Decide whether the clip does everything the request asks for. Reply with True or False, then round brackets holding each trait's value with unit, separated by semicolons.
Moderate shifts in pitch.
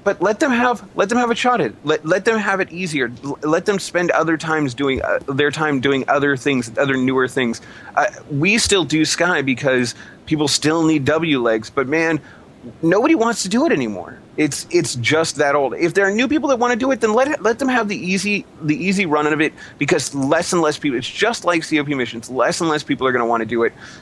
False (5.9 semitones)